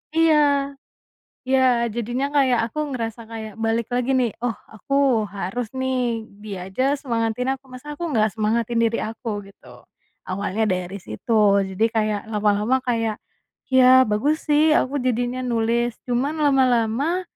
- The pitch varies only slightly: No, average, 3.2 semitones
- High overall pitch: Yes, high, 235 Hz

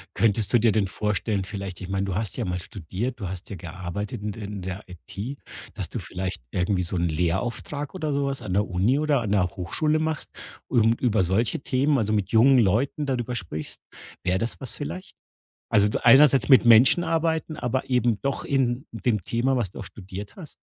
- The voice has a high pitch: No, low, 110 Hz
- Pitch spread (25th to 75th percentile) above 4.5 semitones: Yes, wide, 5.5 semitones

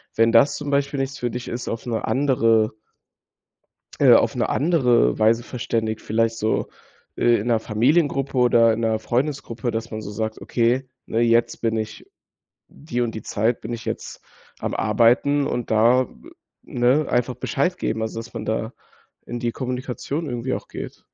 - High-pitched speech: No, low, 120 Hz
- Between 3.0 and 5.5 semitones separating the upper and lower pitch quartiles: No, narrow, 2.4 semitones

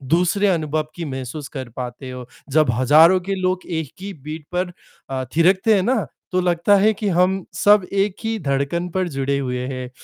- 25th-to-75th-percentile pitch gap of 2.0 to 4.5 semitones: No, wide, 5.4 semitones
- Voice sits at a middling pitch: Yes, medium, 170 Hz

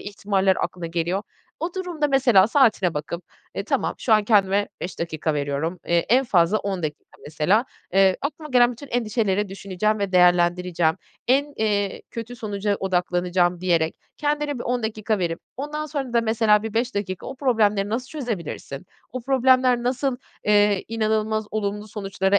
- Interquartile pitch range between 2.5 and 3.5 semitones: No, average, 5.1 semitones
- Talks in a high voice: Yes, high, 210 Hz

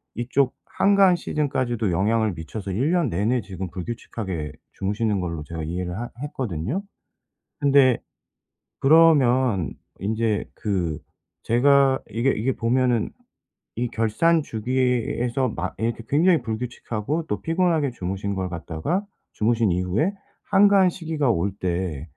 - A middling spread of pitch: No, wide, 6.5 semitones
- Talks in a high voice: No, low, 115 Hz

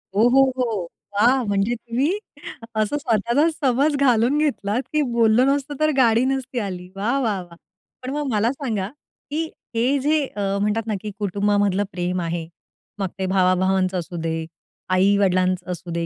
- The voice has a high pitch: Yes, high, 215 Hz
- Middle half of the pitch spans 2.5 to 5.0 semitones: No, wide, 5.5 semitones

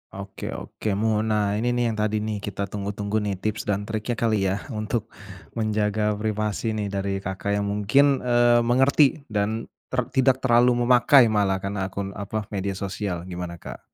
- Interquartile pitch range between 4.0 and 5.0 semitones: No, average, 2.8 semitones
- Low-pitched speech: Yes, low, 105 Hz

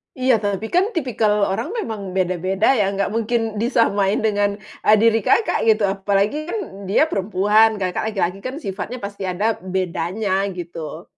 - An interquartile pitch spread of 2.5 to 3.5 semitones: Yes, average, 2.8 semitones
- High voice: Yes, high, 205 Hz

